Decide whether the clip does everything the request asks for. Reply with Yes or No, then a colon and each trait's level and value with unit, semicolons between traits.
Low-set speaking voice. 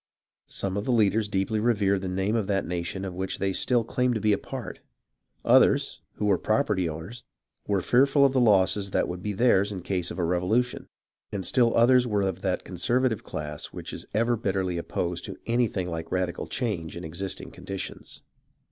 Yes: low, 100 Hz